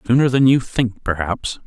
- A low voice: Yes, low, 115 Hz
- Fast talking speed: No, average, 180 wpm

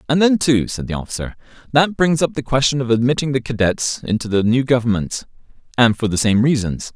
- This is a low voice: Yes, low, 125 Hz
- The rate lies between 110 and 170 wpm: No, average, 200 wpm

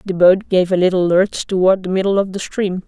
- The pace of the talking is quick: Yes, fast, 250 wpm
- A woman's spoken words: Yes, female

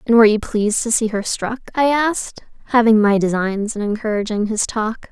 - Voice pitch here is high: Yes, high, 220 Hz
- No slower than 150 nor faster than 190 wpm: No, average, 200 wpm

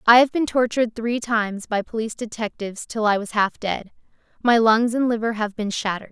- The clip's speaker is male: No, female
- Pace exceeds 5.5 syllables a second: Yes, 5.8 syllables/s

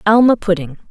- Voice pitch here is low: No, high, 195 Hz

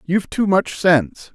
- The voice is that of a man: Yes, male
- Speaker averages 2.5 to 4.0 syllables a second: No, 4.8 syllables/s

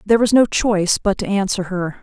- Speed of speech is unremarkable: No, fast, 235 wpm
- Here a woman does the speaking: Yes, female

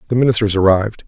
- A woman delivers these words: No, male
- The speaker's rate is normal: Yes, average, 165 wpm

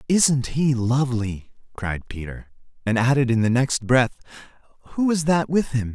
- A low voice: Yes, low, 130 Hz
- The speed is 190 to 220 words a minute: No, average, 160 wpm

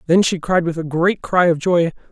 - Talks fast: Yes, fast, 255 wpm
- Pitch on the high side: No, medium, 170 Hz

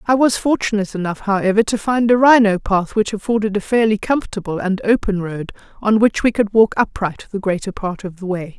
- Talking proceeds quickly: Yes, fast, 210 wpm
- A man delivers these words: No, female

